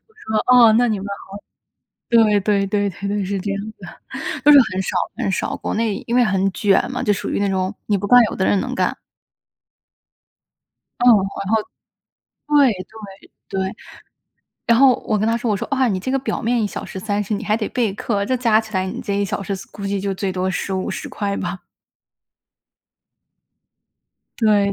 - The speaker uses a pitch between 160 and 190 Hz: No, high, 205 Hz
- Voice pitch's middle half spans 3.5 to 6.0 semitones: No, average, 2.8 semitones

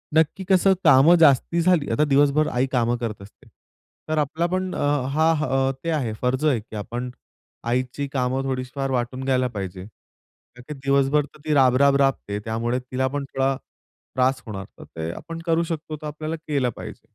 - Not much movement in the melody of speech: No, average, 3.5 semitones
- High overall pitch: No, low, 135 Hz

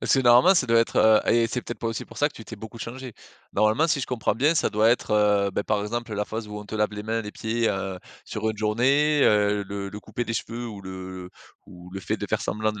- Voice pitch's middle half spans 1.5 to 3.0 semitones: Yes, narrow, 2.4 semitones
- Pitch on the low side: Yes, low, 110 Hz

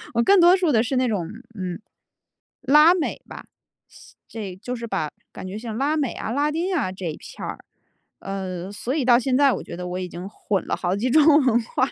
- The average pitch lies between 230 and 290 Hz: Yes, high, 235 Hz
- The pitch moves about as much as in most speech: No, wide, 6.7 semitones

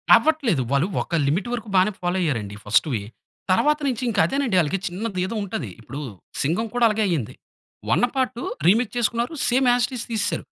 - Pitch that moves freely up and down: Yes, wide, 6.6 semitones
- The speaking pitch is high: Yes, high, 210 Hz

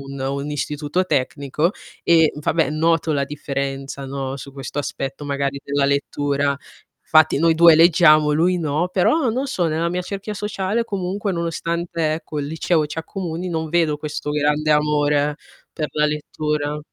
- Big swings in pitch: No, average, 2.8 semitones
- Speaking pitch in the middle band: Yes, medium, 150 Hz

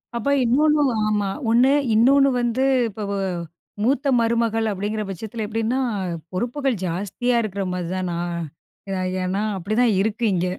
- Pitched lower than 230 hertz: Yes, high, 220 Hz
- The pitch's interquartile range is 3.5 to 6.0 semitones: Yes, average, 3.8 semitones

